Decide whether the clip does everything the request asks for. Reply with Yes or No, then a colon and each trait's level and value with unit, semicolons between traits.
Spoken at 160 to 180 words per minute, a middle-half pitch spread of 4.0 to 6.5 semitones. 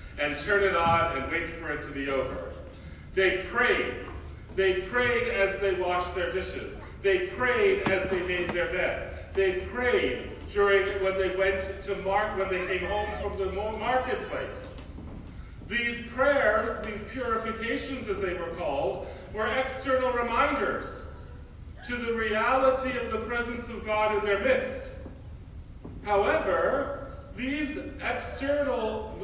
No: average, 140 wpm; average, 5.0 semitones